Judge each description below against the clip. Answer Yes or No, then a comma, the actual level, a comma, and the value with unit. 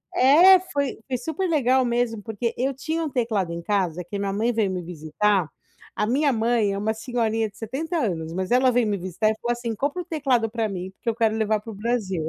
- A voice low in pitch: No, high, 225 Hz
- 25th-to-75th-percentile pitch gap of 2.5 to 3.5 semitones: No, average, 4.2 semitones